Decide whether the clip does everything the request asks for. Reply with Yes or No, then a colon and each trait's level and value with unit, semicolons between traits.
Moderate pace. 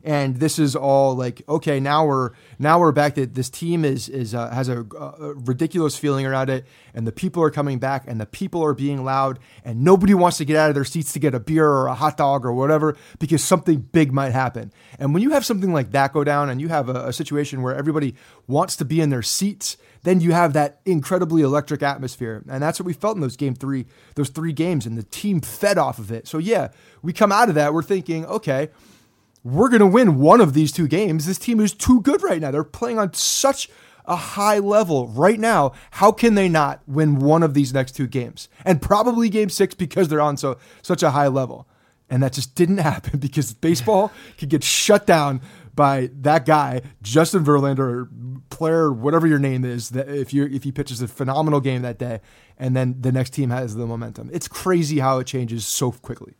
No: fast, 230 wpm